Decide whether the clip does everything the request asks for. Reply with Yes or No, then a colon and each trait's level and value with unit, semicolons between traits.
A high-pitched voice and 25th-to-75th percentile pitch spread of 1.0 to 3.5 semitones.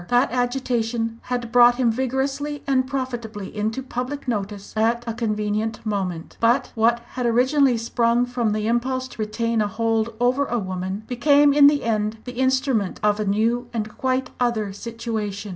Yes: high, 235 Hz; average, 2.8 semitones